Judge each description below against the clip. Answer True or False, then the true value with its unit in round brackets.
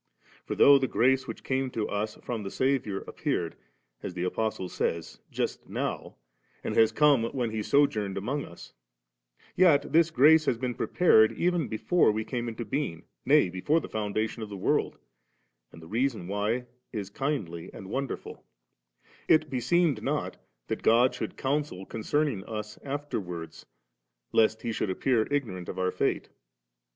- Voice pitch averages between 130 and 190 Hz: False (115 Hz)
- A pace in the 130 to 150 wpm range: False (160 wpm)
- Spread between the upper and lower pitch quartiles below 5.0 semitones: False (5.3 semitones)